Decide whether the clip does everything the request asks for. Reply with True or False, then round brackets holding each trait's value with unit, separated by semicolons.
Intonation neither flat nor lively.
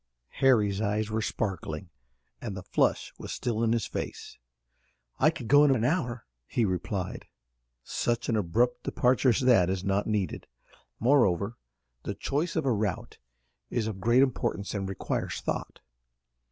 True (3.9 semitones)